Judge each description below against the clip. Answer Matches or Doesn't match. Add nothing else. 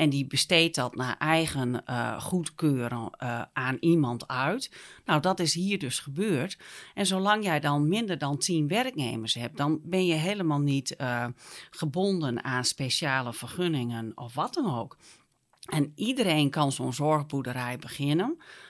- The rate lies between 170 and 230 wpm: Doesn't match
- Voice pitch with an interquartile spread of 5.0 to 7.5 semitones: Matches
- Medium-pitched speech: Matches